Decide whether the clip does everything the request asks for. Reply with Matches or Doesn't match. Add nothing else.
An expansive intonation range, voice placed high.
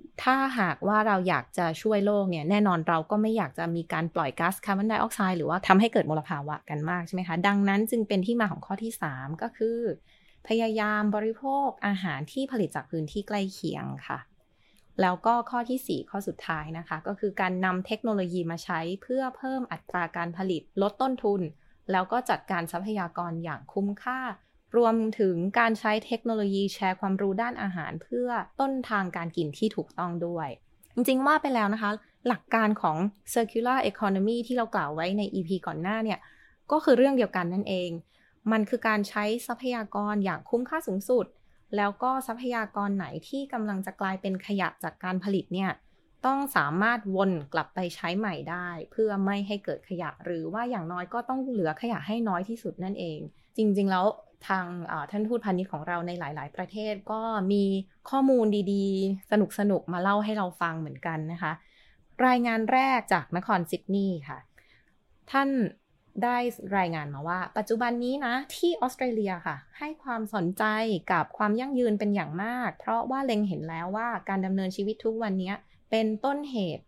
Doesn't match